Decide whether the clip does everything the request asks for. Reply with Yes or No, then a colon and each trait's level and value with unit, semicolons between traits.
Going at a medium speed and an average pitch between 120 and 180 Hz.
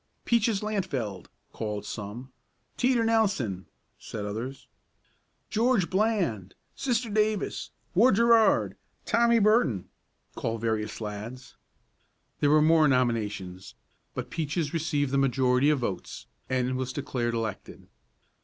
No: slow, 110 wpm; low, 135 Hz